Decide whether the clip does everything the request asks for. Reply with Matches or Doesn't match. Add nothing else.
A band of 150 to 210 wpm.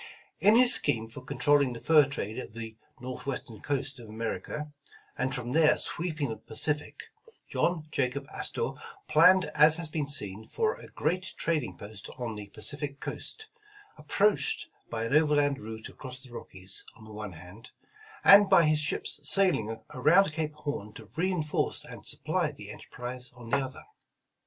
Matches